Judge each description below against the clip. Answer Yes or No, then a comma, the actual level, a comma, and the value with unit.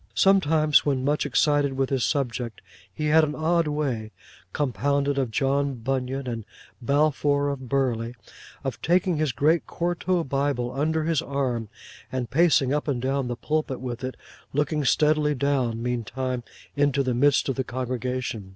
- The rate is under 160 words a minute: Yes, average, 150 wpm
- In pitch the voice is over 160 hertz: No, medium, 140 Hz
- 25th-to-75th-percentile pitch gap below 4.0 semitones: Yes, average, 2.9 semitones